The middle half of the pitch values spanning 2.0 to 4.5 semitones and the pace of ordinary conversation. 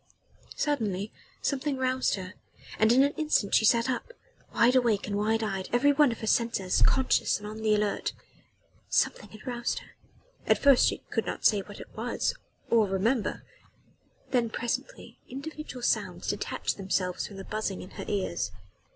Yes: average, 4.1 semitones; average, 170 wpm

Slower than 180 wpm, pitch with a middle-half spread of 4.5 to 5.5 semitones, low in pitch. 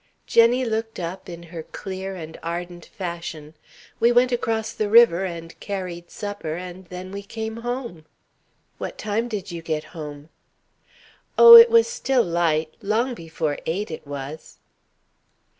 No: average, 145 wpm; average, 5.1 semitones; medium, 185 Hz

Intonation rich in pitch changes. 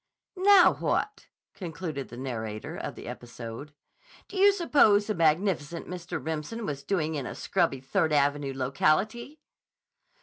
Yes: wide, 7.1 semitones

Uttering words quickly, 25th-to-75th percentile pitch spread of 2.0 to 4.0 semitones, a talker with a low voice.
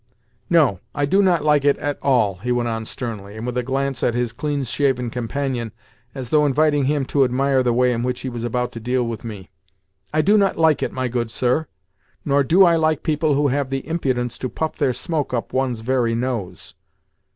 Yes: fast, 220 wpm; average, 3.3 semitones; low, 130 Hz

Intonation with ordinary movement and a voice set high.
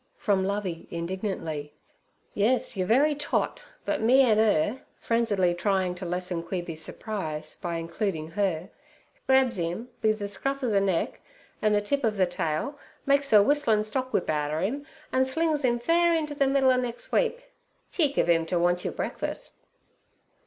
No: wide, 6.9 semitones; high, 210 Hz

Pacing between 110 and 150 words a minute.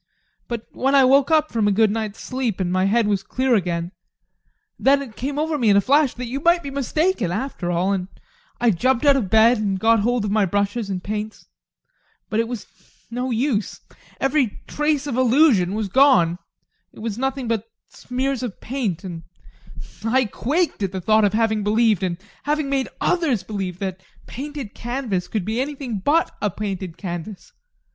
No: average, 190 wpm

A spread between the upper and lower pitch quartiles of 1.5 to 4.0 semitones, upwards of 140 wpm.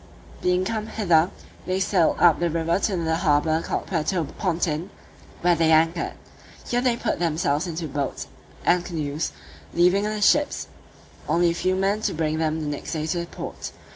Yes: average, 2.8 semitones; average, 175 wpm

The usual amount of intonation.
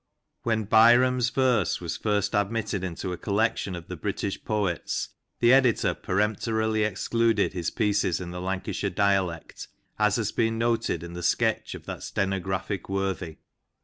Yes: average, 3.2 semitones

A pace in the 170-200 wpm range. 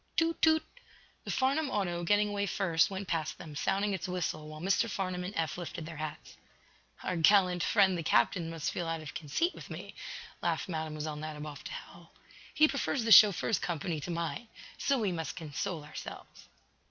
Yes: average, 180 wpm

